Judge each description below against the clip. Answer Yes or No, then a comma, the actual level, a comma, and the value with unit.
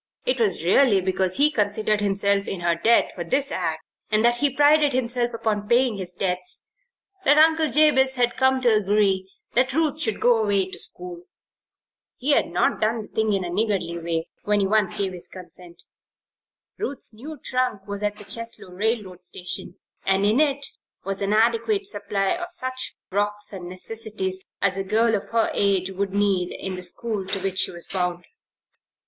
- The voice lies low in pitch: No, high, 205 Hz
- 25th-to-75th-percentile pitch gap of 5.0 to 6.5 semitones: No, average, 4.2 semitones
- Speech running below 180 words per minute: No, average, 185 wpm